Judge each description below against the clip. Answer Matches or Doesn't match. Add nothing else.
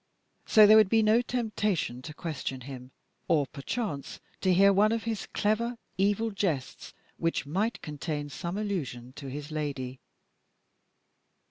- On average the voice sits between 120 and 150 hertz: Doesn't match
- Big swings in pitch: Matches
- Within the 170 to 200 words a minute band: Doesn't match